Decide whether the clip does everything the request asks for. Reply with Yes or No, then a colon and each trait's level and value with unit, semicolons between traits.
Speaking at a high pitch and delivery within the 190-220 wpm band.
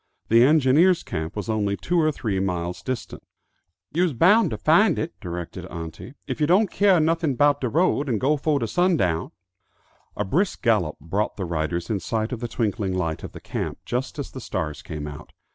No: low, 120 Hz; average, 200 wpm